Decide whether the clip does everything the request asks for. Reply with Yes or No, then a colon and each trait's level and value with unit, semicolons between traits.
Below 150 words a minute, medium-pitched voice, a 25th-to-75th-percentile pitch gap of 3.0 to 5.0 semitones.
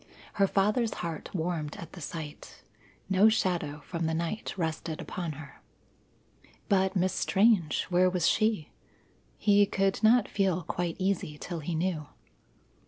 Yes: average, 140 wpm; medium, 180 Hz; average, 3.4 semitones